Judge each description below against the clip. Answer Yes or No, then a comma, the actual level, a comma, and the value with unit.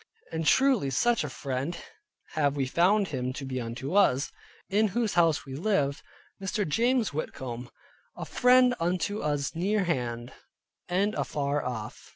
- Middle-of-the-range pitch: Yes, medium, 155 Hz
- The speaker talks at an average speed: Yes, average, 155 wpm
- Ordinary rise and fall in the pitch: No, wide, 7.2 semitones